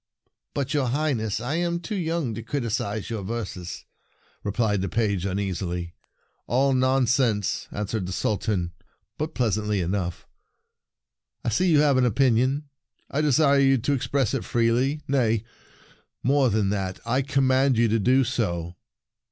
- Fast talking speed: No, average, 150 wpm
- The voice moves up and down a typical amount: Yes, average, 5.0 semitones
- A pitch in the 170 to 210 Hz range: No, low, 120 Hz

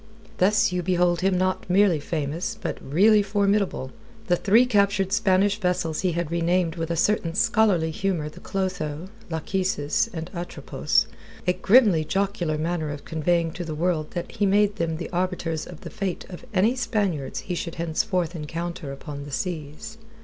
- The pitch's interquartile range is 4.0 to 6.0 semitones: No, average, 3.4 semitones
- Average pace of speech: Yes, average, 165 wpm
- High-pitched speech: No, medium, 175 Hz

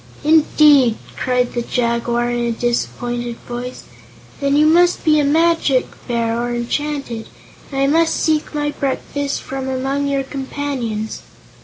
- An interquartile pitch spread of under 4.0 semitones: Yes, average, 3.5 semitones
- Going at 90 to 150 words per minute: Yes, average, 140 wpm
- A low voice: No, very high, 270 Hz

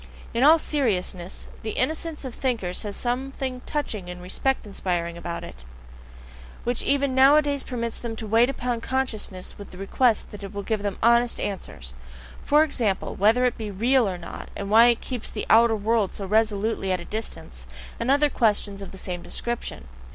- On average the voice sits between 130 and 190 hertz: No, high, 225 Hz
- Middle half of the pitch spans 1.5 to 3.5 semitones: No, average, 4.5 semitones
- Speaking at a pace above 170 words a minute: Yes, average, 180 wpm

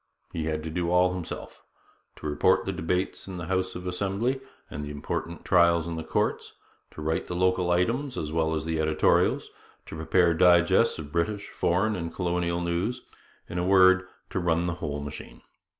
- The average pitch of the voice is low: Yes, very low, 85 Hz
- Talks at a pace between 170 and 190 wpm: Yes, average, 180 wpm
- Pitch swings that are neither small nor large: No, narrow, 2.3 semitones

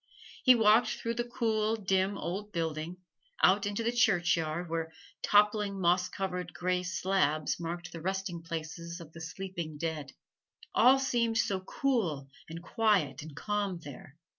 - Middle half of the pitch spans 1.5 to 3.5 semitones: No, average, 4.1 semitones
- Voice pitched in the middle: Yes, medium, 180 Hz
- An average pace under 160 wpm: Yes, average, 145 wpm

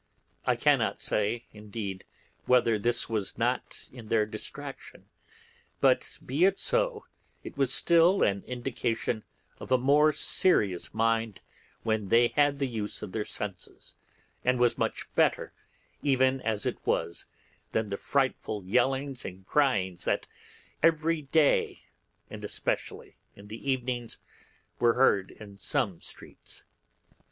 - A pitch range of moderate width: Yes, average, 4.5 semitones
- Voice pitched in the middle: No, low, 120 Hz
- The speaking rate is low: Yes, slow, 130 wpm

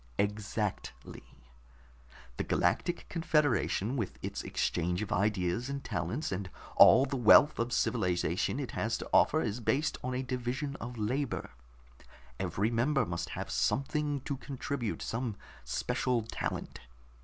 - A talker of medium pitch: No, low, 120 Hz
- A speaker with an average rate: No, slow, 130 wpm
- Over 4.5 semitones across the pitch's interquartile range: Yes, average, 5.2 semitones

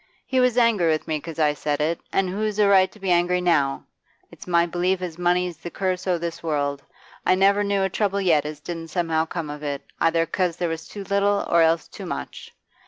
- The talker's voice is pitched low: No, medium, 175 Hz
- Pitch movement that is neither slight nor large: Yes, average, 3.0 semitones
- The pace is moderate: No, fast, 230 wpm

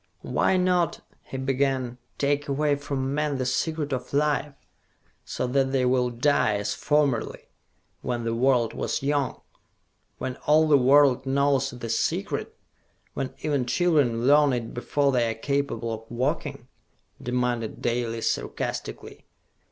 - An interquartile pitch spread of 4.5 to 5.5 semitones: No, average, 2.8 semitones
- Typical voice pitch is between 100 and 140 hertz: Yes, low, 135 Hz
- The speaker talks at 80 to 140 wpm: Yes, slow, 135 wpm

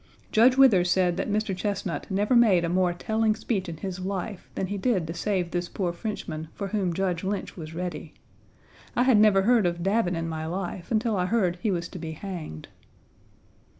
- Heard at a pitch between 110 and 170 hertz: No, high, 190 Hz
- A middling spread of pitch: Yes, average, 3.4 semitones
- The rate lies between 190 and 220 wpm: Yes, average, 200 wpm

